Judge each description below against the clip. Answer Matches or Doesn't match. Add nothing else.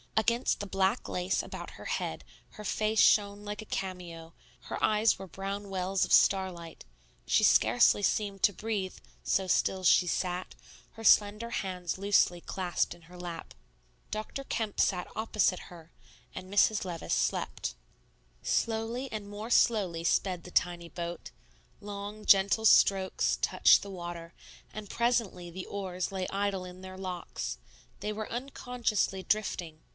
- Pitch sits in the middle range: Doesn't match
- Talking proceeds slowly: Doesn't match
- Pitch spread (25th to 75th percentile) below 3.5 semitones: Matches